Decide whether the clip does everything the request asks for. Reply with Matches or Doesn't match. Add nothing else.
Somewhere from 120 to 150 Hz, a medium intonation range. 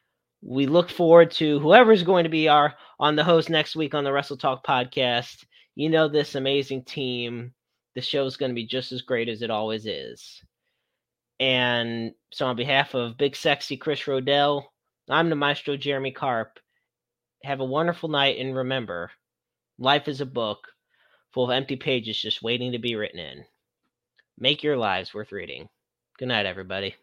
Matches